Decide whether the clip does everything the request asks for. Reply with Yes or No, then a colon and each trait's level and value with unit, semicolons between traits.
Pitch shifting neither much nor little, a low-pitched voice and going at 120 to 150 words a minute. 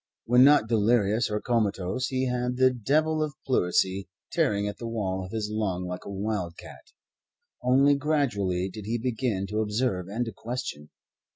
No: average, 4.4 semitones; low, 110 Hz; average, 170 wpm